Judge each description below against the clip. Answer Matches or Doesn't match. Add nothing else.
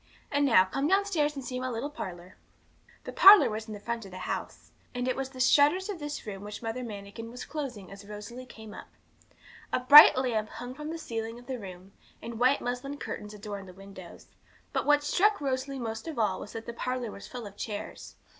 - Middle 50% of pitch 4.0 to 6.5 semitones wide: Matches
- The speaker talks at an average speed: Doesn't match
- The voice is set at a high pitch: Matches